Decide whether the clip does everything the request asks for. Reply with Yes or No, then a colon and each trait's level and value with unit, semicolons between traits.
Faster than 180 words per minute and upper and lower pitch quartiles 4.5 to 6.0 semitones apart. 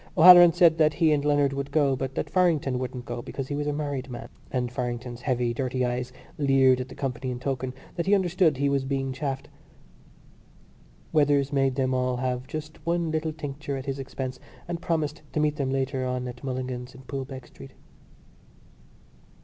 No: average, 190 wpm; average, 2.7 semitones